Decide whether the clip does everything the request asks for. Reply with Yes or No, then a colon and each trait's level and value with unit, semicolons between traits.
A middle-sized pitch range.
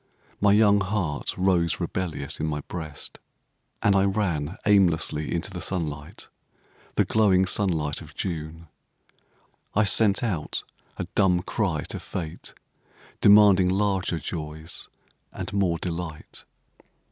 Yes: average, 3.9 semitones